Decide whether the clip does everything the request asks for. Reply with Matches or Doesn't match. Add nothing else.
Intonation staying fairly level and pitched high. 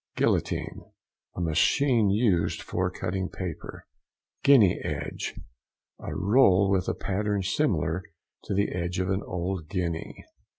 Doesn't match